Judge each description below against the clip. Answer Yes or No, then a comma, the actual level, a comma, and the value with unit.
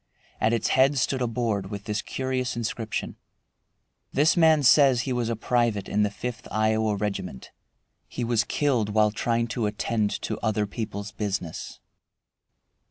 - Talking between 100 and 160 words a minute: Yes, average, 155 wpm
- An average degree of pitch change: Yes, average, 3.0 semitones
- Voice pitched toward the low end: Yes, low, 115 Hz